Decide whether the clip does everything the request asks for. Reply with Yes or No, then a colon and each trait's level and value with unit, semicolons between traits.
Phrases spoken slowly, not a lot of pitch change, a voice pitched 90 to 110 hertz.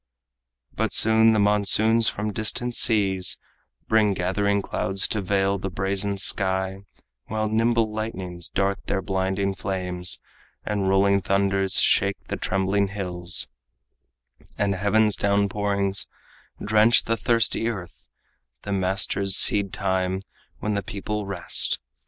Yes: slow, 120 wpm; narrow, 1.8 semitones; low, 100 Hz